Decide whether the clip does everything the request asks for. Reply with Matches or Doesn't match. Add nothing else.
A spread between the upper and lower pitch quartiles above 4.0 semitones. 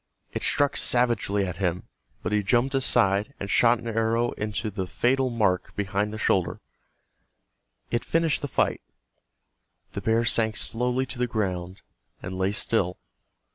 Doesn't match